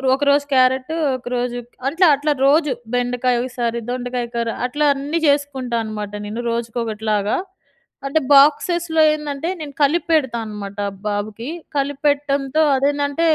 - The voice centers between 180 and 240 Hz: No, very high, 265 Hz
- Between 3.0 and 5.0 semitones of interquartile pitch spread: Yes, average, 3.4 semitones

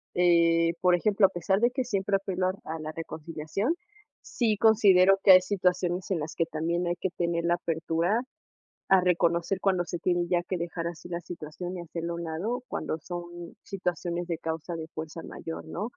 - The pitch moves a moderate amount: No, narrow, 2.3 semitones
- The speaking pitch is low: No, medium, 175 Hz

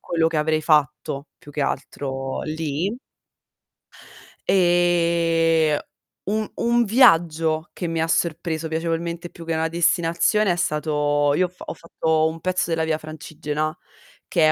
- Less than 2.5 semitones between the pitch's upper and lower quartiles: Yes, narrow, 1.8 semitones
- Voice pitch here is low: No, medium, 165 Hz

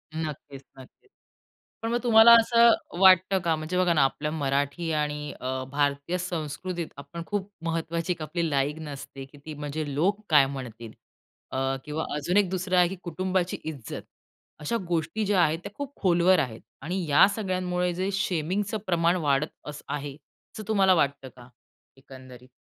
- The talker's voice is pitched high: No, medium, 160 Hz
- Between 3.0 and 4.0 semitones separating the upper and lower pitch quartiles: No, average, 4.5 semitones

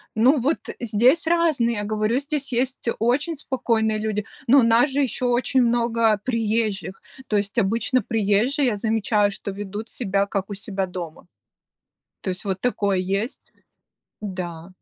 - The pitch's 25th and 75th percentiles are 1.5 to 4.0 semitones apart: Yes, average, 3.6 semitones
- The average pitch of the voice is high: Yes, high, 220 Hz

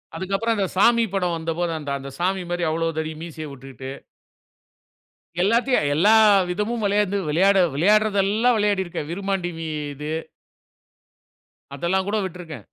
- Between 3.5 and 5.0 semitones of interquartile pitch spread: Yes, average, 4.2 semitones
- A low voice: No, medium, 185 Hz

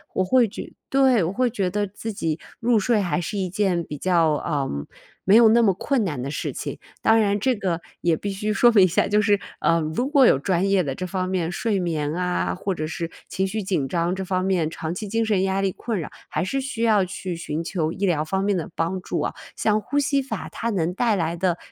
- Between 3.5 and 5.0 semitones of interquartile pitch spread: Yes, average, 3.9 semitones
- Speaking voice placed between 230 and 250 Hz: No, high, 190 Hz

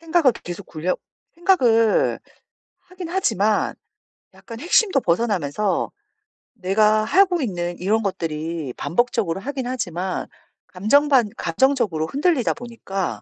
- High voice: Yes, high, 220 Hz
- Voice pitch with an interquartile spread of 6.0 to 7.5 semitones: Yes, wide, 7.1 semitones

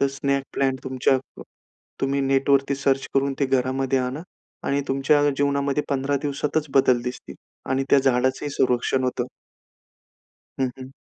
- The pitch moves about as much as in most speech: No, narrow, 1.0 semitones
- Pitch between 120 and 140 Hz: Yes, low, 135 Hz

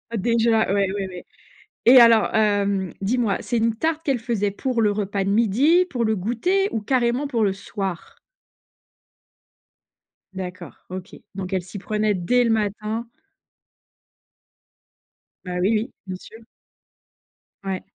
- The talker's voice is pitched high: Yes, high, 215 Hz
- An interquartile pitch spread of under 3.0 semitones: No, average, 3.4 semitones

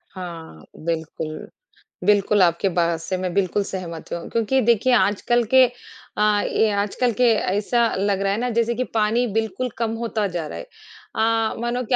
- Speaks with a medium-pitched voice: No, high, 210 Hz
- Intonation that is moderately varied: Yes, average, 4.2 semitones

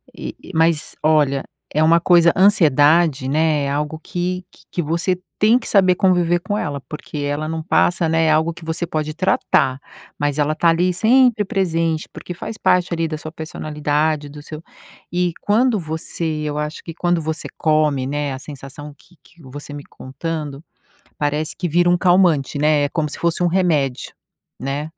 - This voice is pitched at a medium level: Yes, medium, 160 Hz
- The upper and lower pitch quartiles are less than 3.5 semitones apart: Yes, average, 2.9 semitones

